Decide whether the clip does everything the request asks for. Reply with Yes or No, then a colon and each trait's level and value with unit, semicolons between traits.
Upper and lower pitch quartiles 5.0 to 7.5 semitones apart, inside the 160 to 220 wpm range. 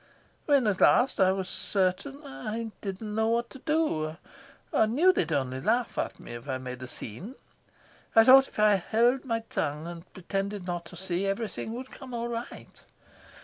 Yes: wide, 5.4 semitones; average, 180 wpm